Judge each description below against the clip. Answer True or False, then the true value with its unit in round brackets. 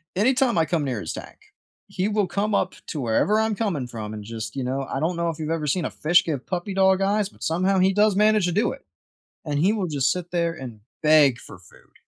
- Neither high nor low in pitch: True (170 Hz)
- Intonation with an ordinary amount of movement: False (6.0 semitones)